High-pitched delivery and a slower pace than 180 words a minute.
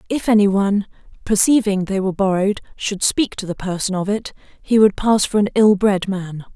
No: high, 200 Hz; average, 200 wpm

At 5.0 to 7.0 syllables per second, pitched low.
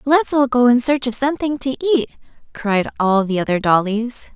No: 5.1 syllables/s; high, 245 Hz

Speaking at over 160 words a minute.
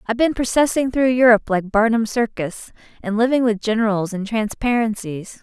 No: average, 155 wpm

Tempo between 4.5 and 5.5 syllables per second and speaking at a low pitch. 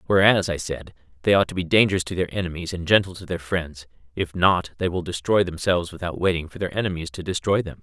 No: 6.3 syllables/s; very low, 90 Hz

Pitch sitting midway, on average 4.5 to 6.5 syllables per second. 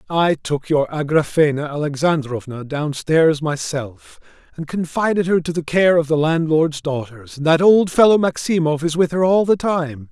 Yes: medium, 155 Hz; 4.6 syllables/s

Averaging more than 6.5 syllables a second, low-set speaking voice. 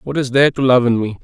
Yes: 6.8 syllables/s; low, 125 Hz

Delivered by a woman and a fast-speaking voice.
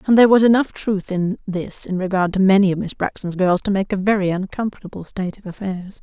Yes: female; fast, 230 wpm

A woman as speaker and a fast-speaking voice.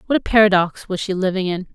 Yes: female; fast, 240 wpm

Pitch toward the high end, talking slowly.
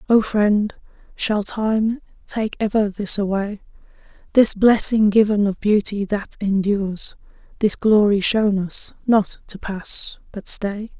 Yes: high, 205 Hz; slow, 130 wpm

